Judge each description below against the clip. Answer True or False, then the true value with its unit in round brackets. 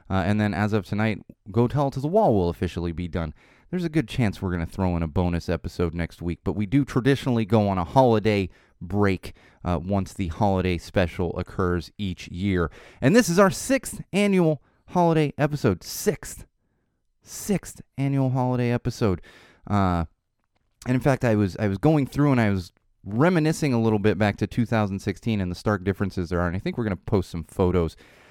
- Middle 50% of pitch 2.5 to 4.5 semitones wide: False (5.6 semitones)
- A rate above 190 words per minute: True (200 wpm)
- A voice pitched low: True (105 Hz)